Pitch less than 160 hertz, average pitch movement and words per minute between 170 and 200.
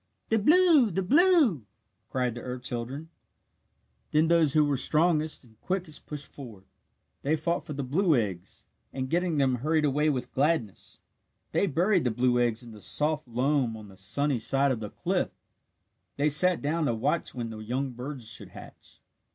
Yes: medium, 140 Hz; average, 4.9 semitones; average, 175 wpm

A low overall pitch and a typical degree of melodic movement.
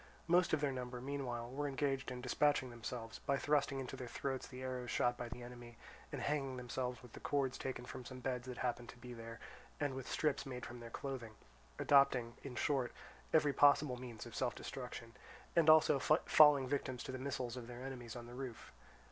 No: low, 130 Hz; narrow, 2.1 semitones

